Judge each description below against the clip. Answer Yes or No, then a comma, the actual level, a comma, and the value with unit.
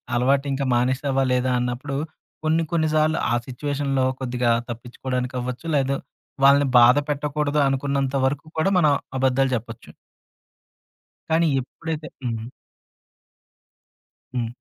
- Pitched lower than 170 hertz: Yes, low, 135 Hz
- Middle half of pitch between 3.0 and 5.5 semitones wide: No, narrow, 2.6 semitones